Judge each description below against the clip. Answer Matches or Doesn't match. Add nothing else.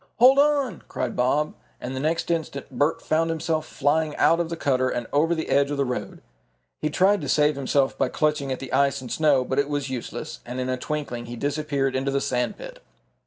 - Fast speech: Matches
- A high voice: Doesn't match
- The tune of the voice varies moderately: Matches